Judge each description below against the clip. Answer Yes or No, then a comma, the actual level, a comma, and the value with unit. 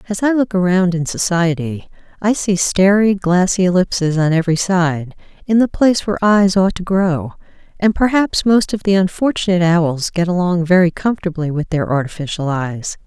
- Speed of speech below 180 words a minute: Yes, average, 165 wpm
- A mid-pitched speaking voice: Yes, medium, 180 Hz